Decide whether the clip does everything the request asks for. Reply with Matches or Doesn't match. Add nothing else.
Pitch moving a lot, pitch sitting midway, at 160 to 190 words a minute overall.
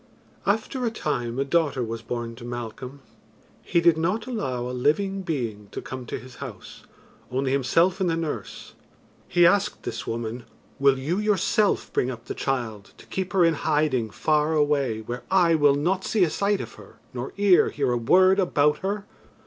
Matches